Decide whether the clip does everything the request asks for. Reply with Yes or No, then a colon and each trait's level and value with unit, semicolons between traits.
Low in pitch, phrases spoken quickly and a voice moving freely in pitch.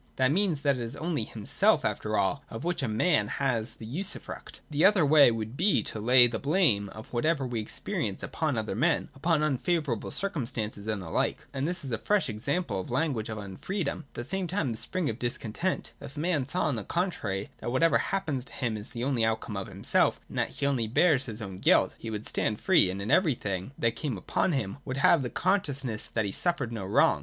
Yes: low, 130 Hz; fast, 230 wpm; wide, 6.7 semitones